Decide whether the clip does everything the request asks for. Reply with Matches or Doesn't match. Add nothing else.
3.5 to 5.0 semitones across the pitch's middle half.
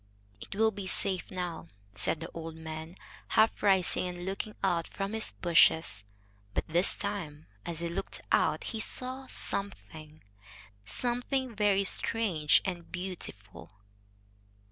Matches